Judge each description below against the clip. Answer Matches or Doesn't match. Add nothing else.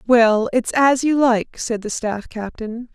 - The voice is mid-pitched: Doesn't match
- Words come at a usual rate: Matches